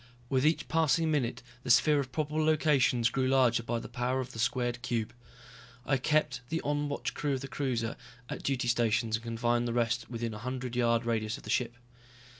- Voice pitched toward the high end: No, low, 125 Hz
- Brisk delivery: Yes, fast, 210 wpm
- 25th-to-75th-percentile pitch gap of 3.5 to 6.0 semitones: No, average, 3.0 semitones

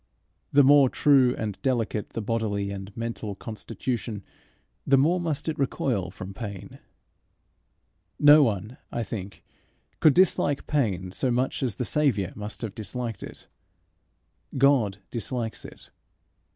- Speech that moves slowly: Yes, slow, 130 wpm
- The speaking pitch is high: No, low, 115 Hz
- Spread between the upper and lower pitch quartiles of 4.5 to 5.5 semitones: Yes, average, 5.1 semitones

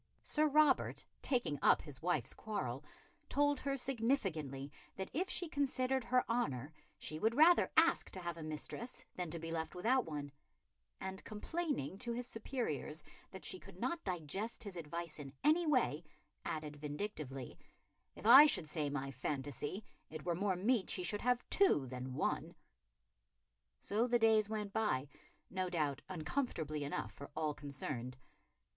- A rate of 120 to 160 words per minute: Yes, average, 155 wpm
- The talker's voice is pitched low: No, medium, 185 Hz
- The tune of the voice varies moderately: No, wide, 8.7 semitones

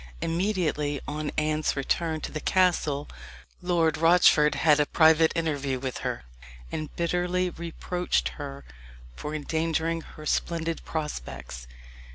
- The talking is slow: Yes, slow, 120 wpm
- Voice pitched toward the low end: No, medium, 160 Hz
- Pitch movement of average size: No, narrow, 2.2 semitones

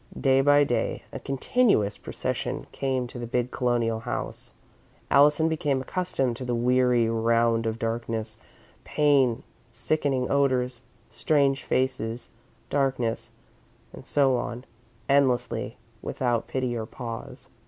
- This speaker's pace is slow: Yes, slow, 120 wpm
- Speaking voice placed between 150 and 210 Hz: No, low, 125 Hz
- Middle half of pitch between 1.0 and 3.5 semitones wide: Yes, average, 2.7 semitones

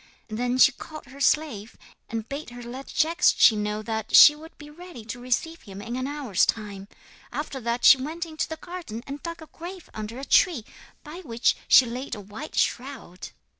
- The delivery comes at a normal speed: Yes, average, 195 wpm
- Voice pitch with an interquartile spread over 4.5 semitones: Yes, wide, 5.4 semitones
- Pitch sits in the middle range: No, very high, 260 Hz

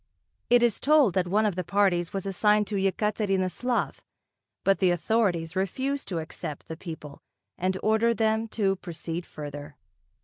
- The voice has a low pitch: No, high, 195 Hz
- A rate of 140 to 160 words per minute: Yes, average, 150 wpm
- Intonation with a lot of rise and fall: No, average, 4.0 semitones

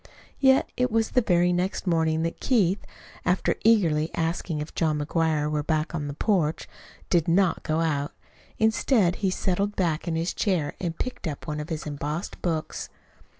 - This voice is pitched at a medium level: Yes, medium, 170 Hz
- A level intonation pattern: No, average, 3.7 semitones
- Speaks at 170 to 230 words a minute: Yes, average, 175 wpm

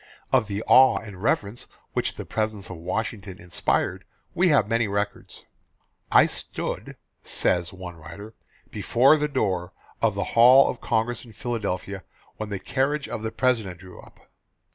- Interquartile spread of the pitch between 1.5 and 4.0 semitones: No, average, 4.4 semitones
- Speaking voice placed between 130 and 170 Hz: No, low, 110 Hz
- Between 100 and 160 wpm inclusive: Yes, average, 155 wpm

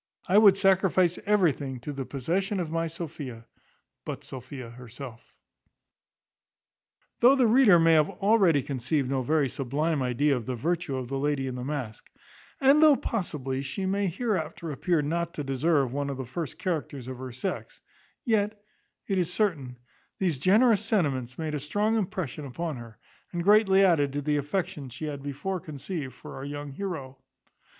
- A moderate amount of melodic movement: No, wide, 5.9 semitones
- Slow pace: No, average, 170 wpm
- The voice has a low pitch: No, medium, 150 Hz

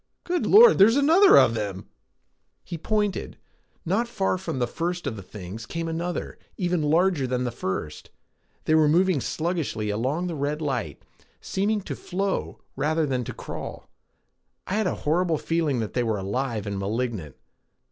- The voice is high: No, medium, 155 Hz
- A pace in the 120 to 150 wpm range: No, average, 165 wpm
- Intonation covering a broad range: Yes, wide, 7.7 semitones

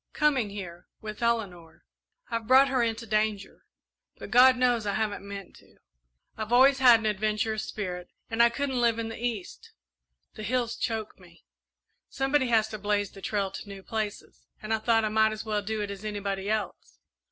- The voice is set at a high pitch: Yes, high, 220 Hz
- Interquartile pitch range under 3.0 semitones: Yes, narrow, 2.4 semitones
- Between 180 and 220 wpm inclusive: Yes, average, 190 wpm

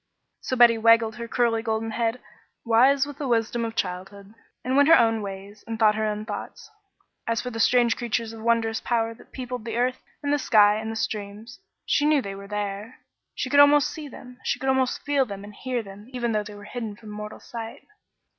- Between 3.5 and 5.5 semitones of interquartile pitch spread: No, average, 2.9 semitones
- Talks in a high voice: Yes, high, 230 Hz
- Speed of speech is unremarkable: No, fast, 215 wpm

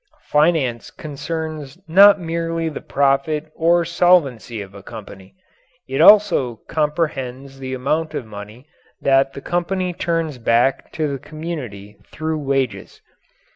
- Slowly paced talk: Yes, slow, 125 wpm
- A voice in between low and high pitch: Yes, medium, 150 Hz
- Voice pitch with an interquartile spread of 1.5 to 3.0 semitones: No, average, 4.5 semitones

